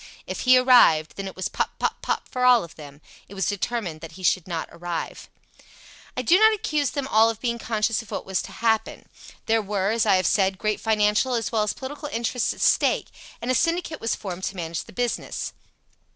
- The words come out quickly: Yes, fast, 220 wpm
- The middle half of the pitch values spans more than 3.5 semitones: Yes, average, 4.6 semitones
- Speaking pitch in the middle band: No, high, 220 Hz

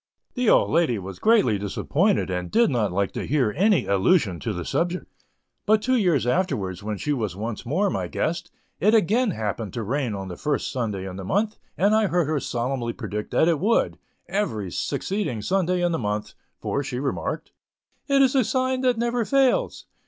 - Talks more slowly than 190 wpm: No, average, 195 wpm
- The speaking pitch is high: No, medium, 145 Hz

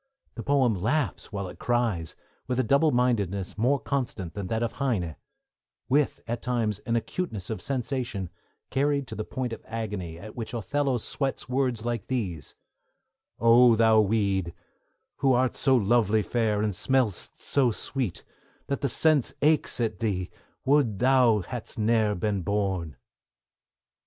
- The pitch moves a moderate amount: Yes, average, 4.0 semitones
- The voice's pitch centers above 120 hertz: No, low, 115 Hz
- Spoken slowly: No, average, 150 wpm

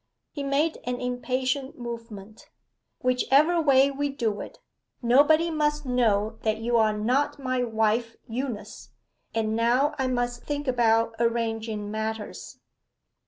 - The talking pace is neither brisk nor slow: No, slow, 125 wpm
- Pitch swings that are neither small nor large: Yes, average, 3.6 semitones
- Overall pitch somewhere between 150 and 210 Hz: No, high, 245 Hz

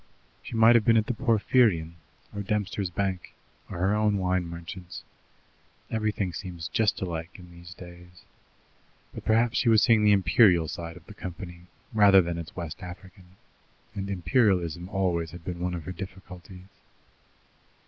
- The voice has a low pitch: Yes, very low, 95 Hz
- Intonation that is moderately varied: Yes, average, 3.2 semitones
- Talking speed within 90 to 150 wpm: No, average, 160 wpm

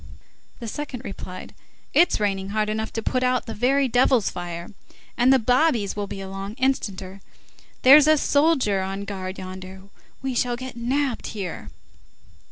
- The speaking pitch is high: Yes, high, 220 Hz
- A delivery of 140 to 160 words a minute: Yes, average, 155 wpm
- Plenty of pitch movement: No, average, 5.0 semitones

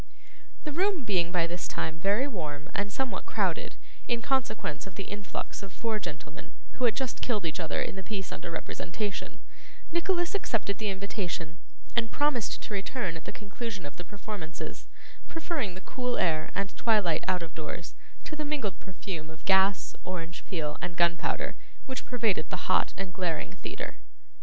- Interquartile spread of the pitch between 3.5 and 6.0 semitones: Yes, wide, 5.5 semitones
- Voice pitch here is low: No, high, 195 Hz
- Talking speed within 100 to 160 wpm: No, average, 170 wpm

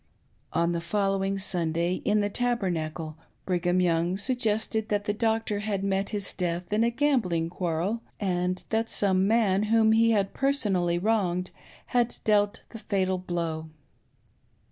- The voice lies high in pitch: Yes, high, 195 Hz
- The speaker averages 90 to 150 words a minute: Yes, average, 145 wpm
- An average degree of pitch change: Yes, average, 3.7 semitones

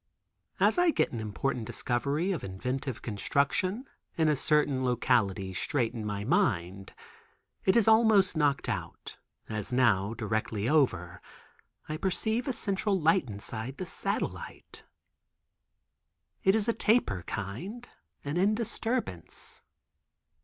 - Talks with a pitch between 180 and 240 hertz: No, low, 135 Hz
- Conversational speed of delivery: No, slow, 125 wpm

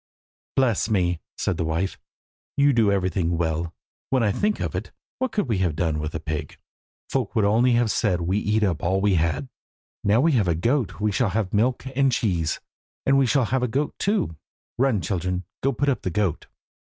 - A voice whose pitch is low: Yes, low, 105 Hz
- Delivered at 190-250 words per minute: Yes, fast, 205 wpm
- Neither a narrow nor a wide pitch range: No, wide, 6.4 semitones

